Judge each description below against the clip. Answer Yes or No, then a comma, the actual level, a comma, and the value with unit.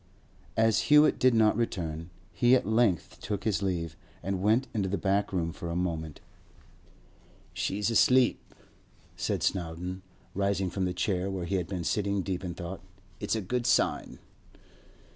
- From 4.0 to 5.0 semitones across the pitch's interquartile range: No, average, 3.6 semitones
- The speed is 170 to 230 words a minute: No, average, 160 wpm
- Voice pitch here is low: Yes, very low, 95 Hz